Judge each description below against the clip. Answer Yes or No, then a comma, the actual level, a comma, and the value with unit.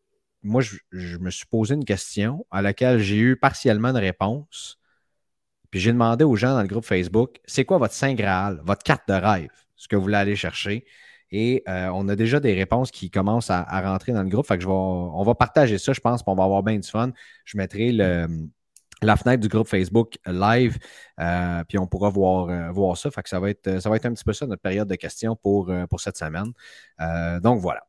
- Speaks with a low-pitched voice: Yes, low, 100 Hz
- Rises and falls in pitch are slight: No, average, 3.9 semitones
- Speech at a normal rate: No, fast, 235 wpm